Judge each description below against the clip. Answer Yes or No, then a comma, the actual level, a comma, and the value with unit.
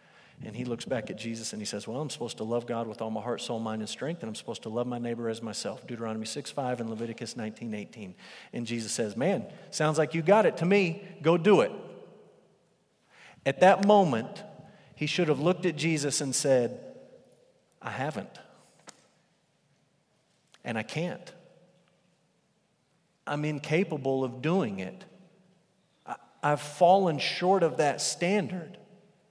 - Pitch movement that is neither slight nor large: No, wide, 7.5 semitones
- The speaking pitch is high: No, medium, 155 Hz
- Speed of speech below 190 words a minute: Yes, average, 165 wpm